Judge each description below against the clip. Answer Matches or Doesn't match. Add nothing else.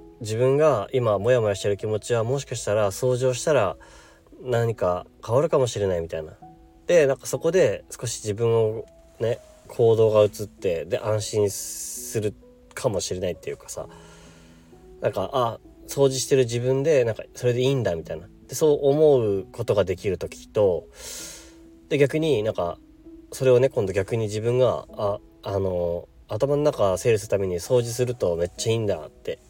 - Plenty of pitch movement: Doesn't match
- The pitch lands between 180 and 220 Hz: Doesn't match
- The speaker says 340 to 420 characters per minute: Doesn't match